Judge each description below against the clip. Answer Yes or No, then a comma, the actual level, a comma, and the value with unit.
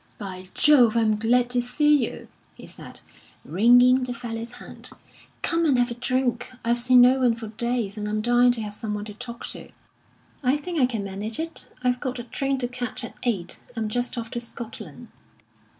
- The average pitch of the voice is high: Yes, high, 240 Hz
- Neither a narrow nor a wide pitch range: No, narrow, 2.1 semitones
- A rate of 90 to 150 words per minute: No, fast, 205 wpm